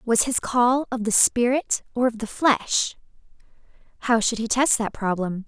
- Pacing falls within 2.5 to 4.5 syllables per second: Yes, 4.3 syllables/s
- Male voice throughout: No, female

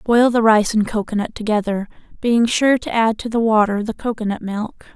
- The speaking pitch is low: No, high, 220 Hz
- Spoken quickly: No, average, 195 wpm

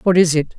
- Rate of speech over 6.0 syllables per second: Yes, 6.3 syllables/s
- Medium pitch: Yes, medium, 170 Hz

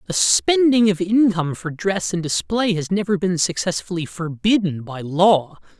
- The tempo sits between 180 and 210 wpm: No, average, 155 wpm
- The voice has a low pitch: No, medium, 180 Hz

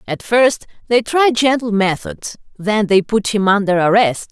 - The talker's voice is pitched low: No, high, 215 Hz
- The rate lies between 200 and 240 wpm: No, average, 165 wpm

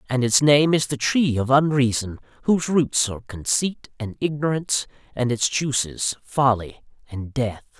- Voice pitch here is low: Yes, low, 130 Hz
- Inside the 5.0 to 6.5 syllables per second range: No, 4.7 syllables/s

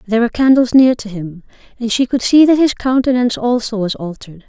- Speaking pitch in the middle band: No, high, 235 Hz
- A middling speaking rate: No, fast, 215 wpm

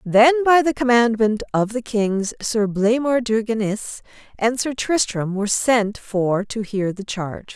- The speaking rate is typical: Yes, average, 165 wpm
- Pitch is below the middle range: No, high, 225 Hz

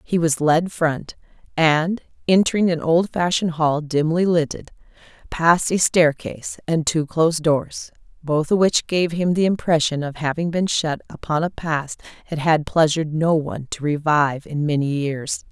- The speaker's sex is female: Yes, female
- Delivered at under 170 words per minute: Yes, average, 160 wpm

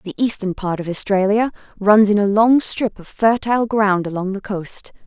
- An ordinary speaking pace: Yes, average, 190 wpm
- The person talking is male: No, female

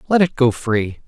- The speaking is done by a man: Yes, male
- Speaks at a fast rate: Yes, fast, 225 wpm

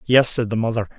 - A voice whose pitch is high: No, low, 115 Hz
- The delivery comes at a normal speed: No, fast, 245 wpm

